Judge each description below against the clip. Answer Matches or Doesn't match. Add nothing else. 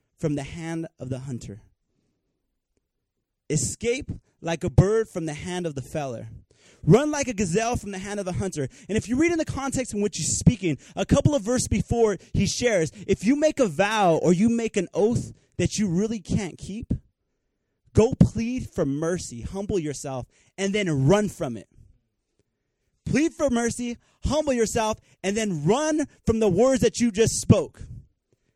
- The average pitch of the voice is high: Matches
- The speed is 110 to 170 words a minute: Doesn't match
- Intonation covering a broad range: Matches